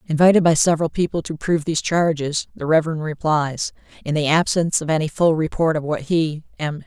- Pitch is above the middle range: No, medium, 155 Hz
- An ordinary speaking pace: Yes, average, 190 wpm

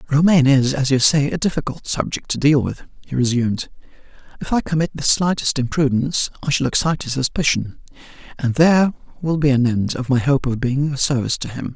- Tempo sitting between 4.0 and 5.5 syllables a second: No, 6.0 syllables/s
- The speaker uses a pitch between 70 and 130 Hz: No, medium, 140 Hz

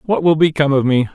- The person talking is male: Yes, male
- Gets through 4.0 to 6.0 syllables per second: No, 6.5 syllables/s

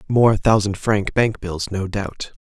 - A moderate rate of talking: Yes, average, 175 wpm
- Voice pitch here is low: Yes, low, 105 Hz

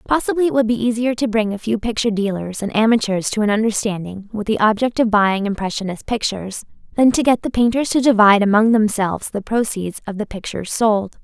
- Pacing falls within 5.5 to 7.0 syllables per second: Yes, 6.0 syllables/s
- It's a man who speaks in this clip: No, female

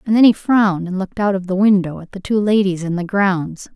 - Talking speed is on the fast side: Yes, fast, 270 wpm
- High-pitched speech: Yes, high, 195 Hz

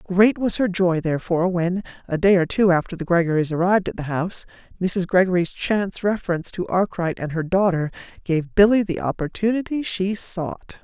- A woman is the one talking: Yes, female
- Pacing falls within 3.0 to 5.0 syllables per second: No, 5.6 syllables/s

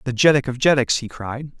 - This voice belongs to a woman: No, male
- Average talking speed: No, fast, 225 wpm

